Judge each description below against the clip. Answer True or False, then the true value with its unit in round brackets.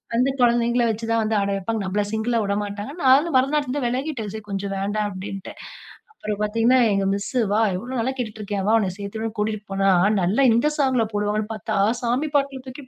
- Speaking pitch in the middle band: False (220 Hz)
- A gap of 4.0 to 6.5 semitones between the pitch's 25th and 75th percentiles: False (3.5 semitones)